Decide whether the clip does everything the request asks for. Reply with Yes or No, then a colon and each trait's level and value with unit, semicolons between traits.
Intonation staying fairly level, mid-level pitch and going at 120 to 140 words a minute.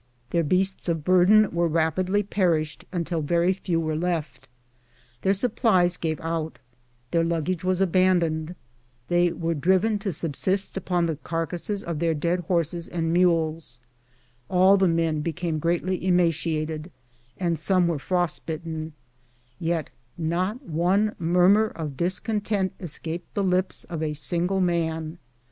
Yes: narrow, 2.3 semitones; medium, 170 Hz; slow, 135 wpm